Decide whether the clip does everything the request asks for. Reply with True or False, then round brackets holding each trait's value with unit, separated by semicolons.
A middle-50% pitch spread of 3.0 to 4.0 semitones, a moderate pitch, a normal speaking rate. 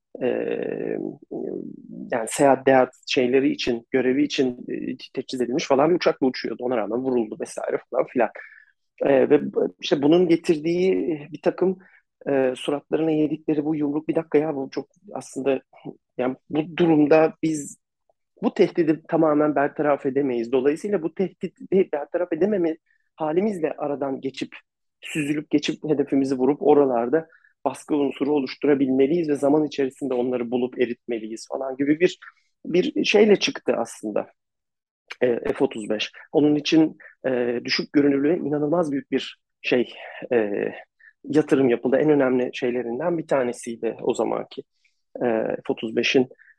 True (3.7 semitones; 145 Hz; 120 wpm)